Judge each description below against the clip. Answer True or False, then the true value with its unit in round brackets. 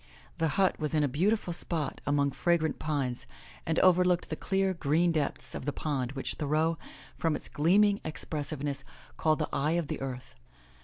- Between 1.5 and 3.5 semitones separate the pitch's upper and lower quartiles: True (3.2 semitones)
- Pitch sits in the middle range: True (155 Hz)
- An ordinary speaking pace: True (170 wpm)